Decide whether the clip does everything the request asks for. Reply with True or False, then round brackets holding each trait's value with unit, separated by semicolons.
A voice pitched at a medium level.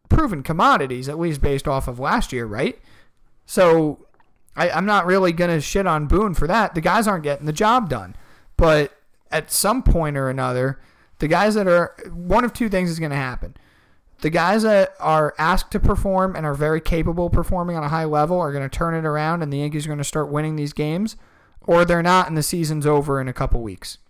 True (155 Hz)